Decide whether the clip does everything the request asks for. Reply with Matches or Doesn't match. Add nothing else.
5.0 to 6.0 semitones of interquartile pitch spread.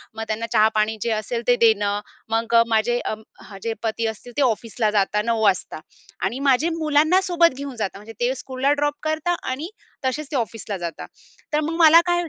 Matches